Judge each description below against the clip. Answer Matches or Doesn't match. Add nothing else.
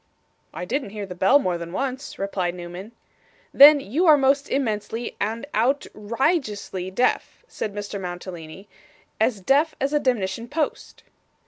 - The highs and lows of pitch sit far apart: Matches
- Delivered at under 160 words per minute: Matches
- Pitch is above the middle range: Matches